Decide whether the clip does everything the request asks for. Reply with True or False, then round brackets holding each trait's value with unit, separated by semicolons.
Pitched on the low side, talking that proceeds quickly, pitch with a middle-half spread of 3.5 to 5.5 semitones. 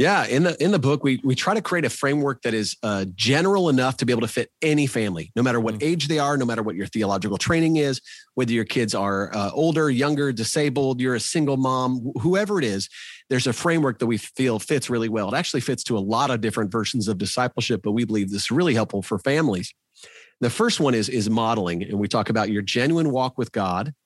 True (125 Hz; 240 wpm; 4.4 semitones)